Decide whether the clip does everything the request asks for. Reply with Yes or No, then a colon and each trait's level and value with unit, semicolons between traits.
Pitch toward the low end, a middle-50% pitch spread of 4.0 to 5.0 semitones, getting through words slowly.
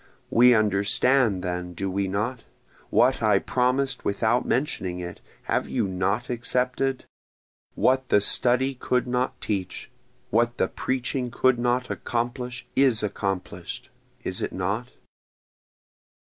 Yes: low, 120 Hz; average, 4.3 semitones; slow, 120 wpm